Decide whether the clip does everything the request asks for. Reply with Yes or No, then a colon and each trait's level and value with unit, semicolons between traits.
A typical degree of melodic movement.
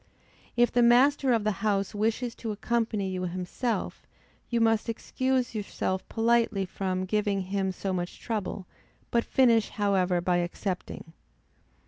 Yes: average, 3.8 semitones